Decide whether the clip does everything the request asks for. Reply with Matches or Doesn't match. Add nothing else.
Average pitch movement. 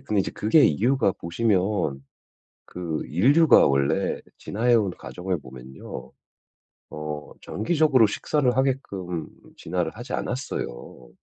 Doesn't match